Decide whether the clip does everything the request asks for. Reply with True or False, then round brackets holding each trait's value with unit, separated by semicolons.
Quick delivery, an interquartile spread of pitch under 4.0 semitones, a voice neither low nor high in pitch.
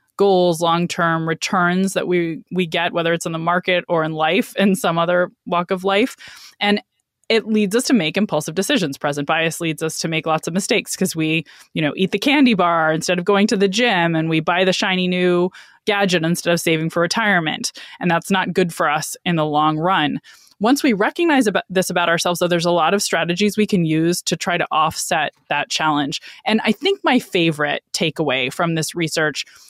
True (215 wpm; 3.4 semitones; 175 Hz)